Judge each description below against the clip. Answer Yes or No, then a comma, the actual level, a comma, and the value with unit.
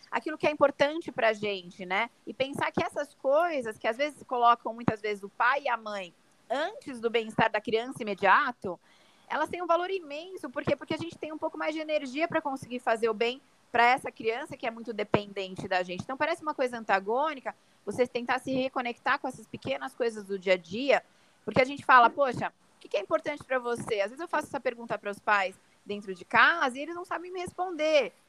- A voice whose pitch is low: No, very high, 255 Hz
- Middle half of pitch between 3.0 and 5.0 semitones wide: No, wide, 5.4 semitones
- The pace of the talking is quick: Yes, fast, 225 wpm